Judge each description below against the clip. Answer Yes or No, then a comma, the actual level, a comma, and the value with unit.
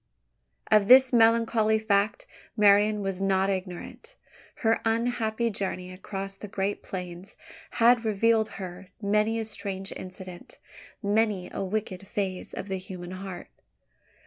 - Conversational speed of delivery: No, slow, 130 wpm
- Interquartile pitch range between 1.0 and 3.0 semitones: Yes, average, 2.7 semitones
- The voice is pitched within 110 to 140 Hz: No, high, 200 Hz